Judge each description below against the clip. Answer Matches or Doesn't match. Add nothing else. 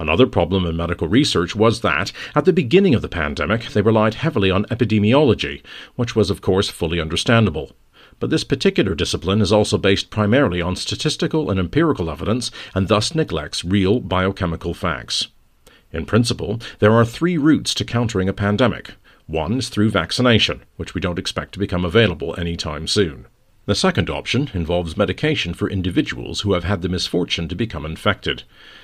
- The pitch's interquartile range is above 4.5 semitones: Matches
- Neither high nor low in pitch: Doesn't match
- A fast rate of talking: Doesn't match